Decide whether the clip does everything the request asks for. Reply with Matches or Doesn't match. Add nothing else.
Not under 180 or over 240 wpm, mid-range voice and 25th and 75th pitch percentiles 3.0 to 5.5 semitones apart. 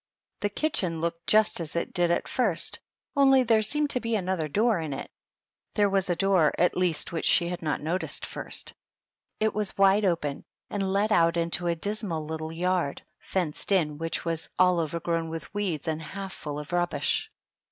Matches